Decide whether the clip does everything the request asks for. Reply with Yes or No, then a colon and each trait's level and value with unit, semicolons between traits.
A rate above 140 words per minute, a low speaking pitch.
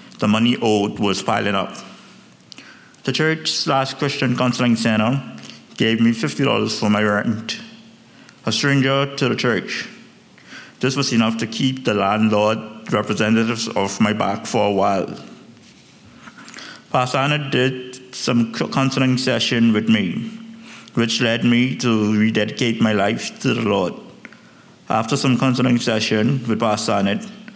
No: slow, 135 wpm; low, 120 Hz